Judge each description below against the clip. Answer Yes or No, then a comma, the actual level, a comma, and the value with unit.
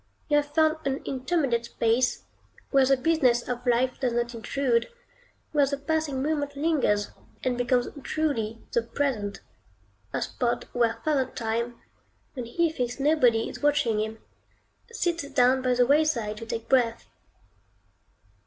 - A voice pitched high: Yes, very high, 255 Hz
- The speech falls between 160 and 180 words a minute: No, average, 145 wpm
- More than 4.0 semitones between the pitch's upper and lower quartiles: No, average, 3.6 semitones